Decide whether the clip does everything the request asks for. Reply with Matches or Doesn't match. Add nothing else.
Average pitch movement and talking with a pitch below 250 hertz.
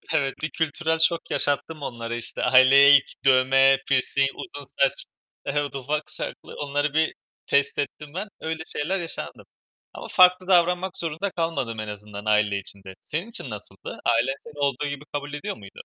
Matches